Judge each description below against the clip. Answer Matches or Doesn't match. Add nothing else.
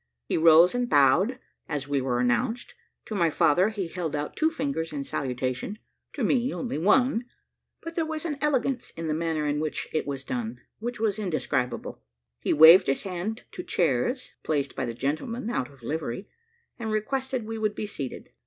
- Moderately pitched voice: Matches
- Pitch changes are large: Matches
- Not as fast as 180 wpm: Doesn't match